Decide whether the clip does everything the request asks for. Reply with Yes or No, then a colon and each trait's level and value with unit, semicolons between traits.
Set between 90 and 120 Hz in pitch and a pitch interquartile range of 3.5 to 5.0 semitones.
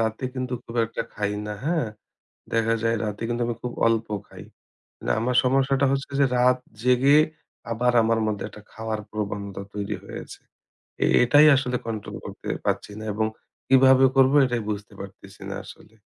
No: low, 115 Hz; average, 3.0 semitones